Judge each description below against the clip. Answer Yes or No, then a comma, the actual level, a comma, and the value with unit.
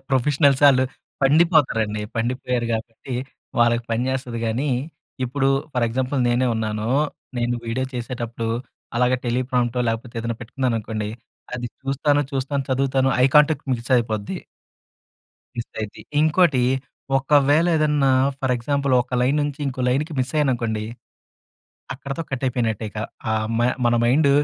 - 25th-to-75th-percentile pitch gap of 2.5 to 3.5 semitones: Yes, average, 2.9 semitones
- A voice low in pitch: Yes, low, 125 Hz